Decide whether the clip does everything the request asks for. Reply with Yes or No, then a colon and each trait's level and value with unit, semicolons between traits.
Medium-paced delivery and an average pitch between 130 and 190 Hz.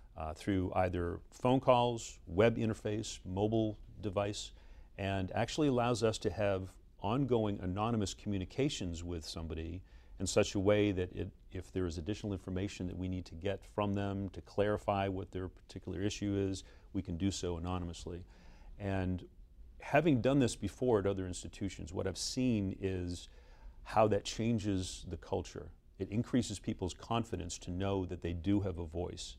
No: average, 160 wpm; very low, 95 Hz